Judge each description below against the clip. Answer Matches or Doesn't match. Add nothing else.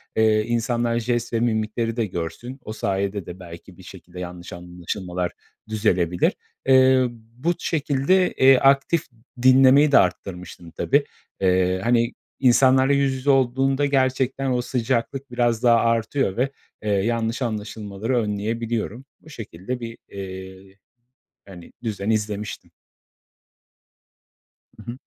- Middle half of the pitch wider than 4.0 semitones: Matches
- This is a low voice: Matches